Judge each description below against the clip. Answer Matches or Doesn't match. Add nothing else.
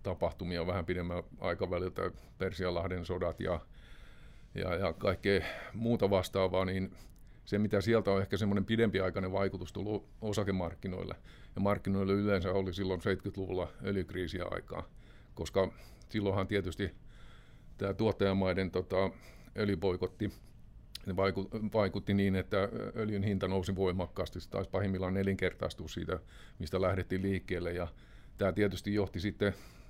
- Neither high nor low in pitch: Doesn't match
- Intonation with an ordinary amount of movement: Doesn't match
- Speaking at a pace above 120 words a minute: Doesn't match